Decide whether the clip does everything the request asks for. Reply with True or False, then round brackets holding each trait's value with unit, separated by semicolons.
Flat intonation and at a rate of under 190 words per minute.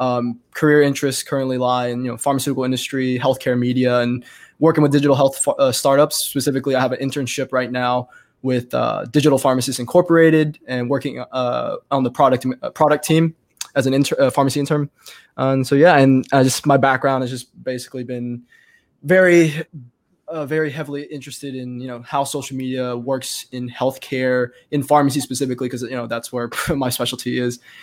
True (2.3 semitones; 180 wpm)